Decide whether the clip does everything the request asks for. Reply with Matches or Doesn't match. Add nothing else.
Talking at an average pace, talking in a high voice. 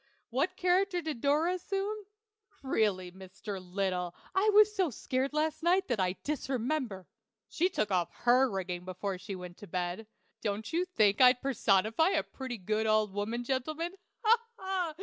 Matches